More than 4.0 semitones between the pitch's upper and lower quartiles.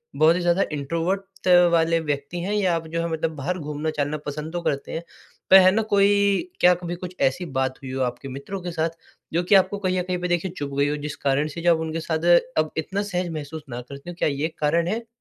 No: average, 3.5 semitones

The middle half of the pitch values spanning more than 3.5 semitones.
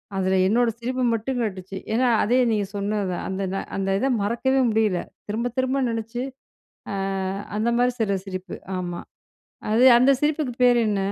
Yes: average, 4.1 semitones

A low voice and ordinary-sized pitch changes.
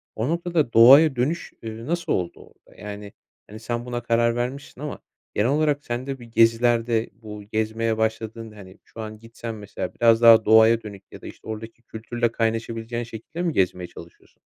No: low, 115 Hz; narrow, 1.7 semitones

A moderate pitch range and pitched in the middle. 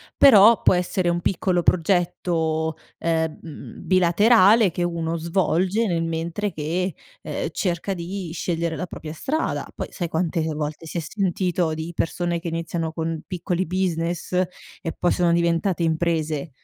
No: narrow, 2.0 semitones; medium, 170 Hz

